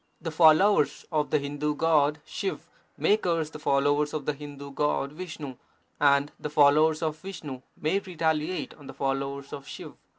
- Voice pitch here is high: No, medium, 150 Hz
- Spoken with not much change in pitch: Yes, narrow, 2.0 semitones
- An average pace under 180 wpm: Yes, average, 165 wpm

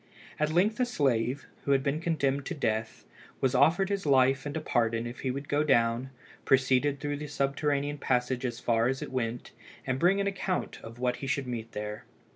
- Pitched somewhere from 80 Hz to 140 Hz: Yes, low, 135 Hz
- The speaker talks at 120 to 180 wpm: No, fast, 205 wpm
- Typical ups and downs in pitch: Yes, average, 3.2 semitones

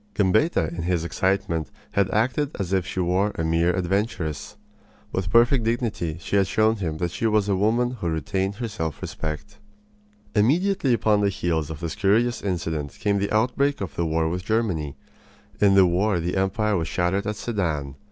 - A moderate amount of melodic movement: Yes, average, 4.3 semitones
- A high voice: No, very low, 95 Hz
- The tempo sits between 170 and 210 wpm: Yes, average, 180 wpm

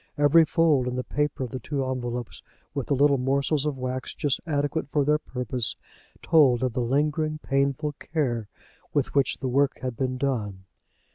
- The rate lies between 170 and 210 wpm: Yes, average, 180 wpm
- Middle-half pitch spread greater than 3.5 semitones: No, narrow, 2.5 semitones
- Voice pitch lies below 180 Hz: Yes, low, 135 Hz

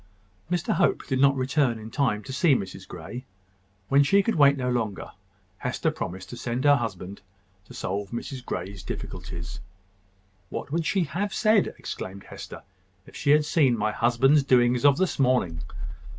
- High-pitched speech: No, low, 130 Hz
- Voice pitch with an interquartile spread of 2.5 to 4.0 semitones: No, wide, 5.4 semitones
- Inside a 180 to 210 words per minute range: No, average, 165 wpm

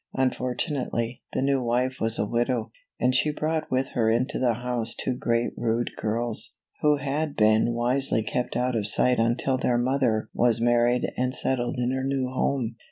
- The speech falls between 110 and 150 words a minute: No, average, 175 wpm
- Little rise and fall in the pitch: Yes, narrow, 2.0 semitones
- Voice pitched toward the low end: Yes, low, 125 Hz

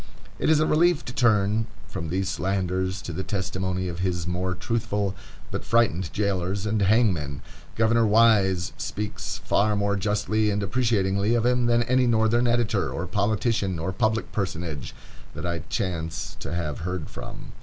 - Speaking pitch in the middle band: No, low, 100 Hz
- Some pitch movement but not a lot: Yes, average, 3.5 semitones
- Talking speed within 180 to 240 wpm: No, average, 160 wpm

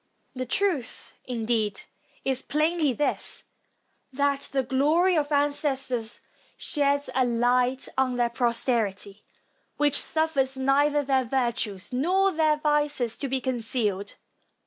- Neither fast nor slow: No, slow, 115 wpm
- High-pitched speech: Yes, very high, 265 Hz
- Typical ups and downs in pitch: Yes, average, 3.4 semitones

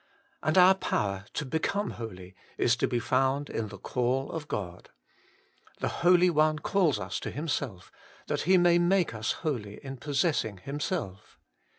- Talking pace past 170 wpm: No, average, 160 wpm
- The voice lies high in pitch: No, medium, 140 Hz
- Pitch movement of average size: No, wide, 7.7 semitones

